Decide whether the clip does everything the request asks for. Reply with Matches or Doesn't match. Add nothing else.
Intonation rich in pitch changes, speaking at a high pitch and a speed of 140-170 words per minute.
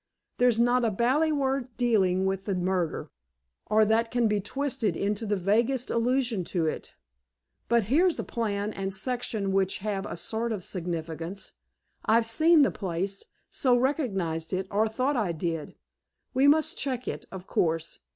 Doesn't match